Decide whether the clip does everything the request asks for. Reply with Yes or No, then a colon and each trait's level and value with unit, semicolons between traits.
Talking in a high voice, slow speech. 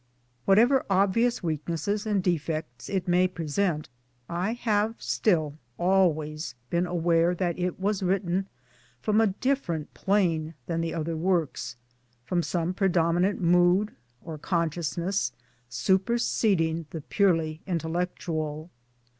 No: medium, 175 Hz; slow, 115 wpm